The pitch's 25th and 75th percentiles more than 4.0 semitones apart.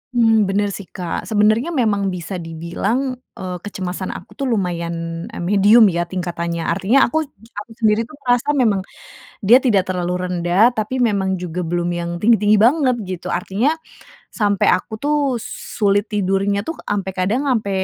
No: average, 3.6 semitones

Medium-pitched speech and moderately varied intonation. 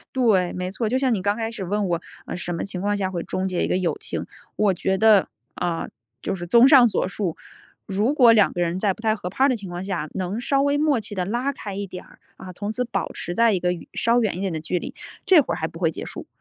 No: high, 200 Hz; average, 4.3 semitones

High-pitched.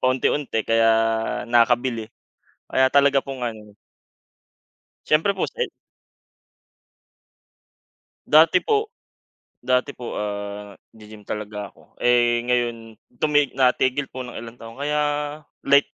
No: low, 120 Hz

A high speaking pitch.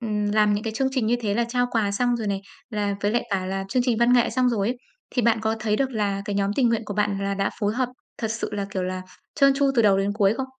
Yes: high, 215 Hz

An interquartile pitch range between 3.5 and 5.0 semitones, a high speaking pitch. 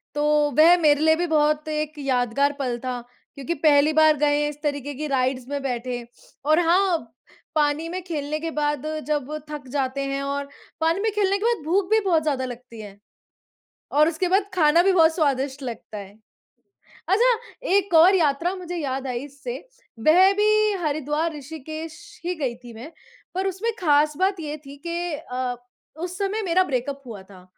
Yes: average, 3.9 semitones; very high, 300 Hz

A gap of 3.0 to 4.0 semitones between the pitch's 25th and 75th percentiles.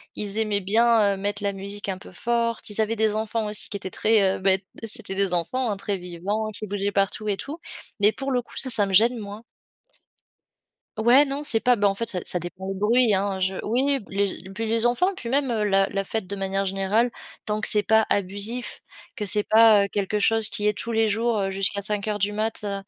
No: narrow, 2.4 semitones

